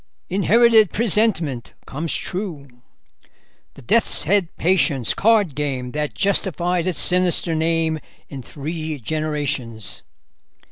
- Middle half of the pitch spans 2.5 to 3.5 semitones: No, average, 4.9 semitones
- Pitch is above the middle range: No, medium, 160 Hz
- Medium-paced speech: No, slow, 100 wpm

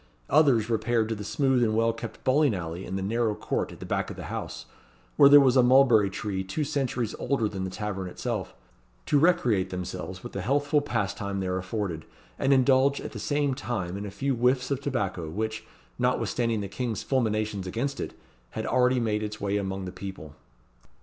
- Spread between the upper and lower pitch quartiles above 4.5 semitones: Yes, average, 5.0 semitones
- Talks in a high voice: No, low, 110 Hz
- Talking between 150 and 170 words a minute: No, average, 195 wpm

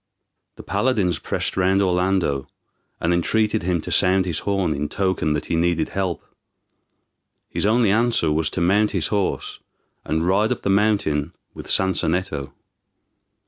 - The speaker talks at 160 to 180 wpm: No, average, 145 wpm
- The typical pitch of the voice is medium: No, very low, 95 Hz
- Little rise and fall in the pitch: No, average, 3.3 semitones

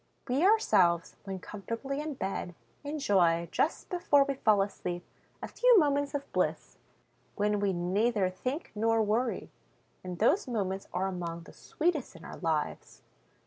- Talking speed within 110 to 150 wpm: Yes, average, 145 wpm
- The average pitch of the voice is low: No, high, 210 Hz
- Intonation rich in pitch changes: Yes, wide, 7.2 semitones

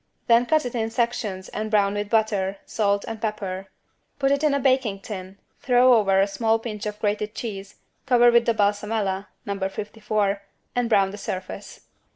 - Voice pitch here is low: No, high, 210 Hz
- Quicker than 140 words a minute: Yes, average, 180 wpm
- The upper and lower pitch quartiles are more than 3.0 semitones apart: No, average, 2.7 semitones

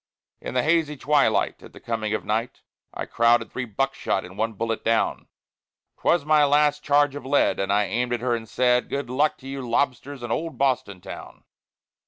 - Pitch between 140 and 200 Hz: No, low, 125 Hz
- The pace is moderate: Yes, average, 190 wpm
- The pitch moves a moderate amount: Yes, average, 4.0 semitones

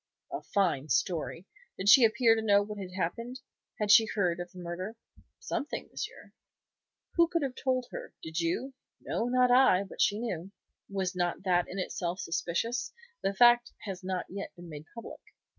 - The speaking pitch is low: No, high, 195 Hz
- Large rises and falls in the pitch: No, average, 4.9 semitones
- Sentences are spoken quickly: No, average, 175 wpm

